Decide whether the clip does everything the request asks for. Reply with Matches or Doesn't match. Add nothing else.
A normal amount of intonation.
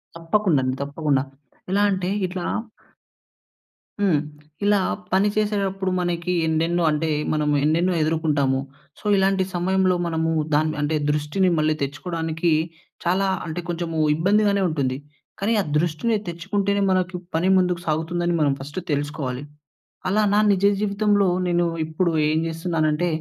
Matches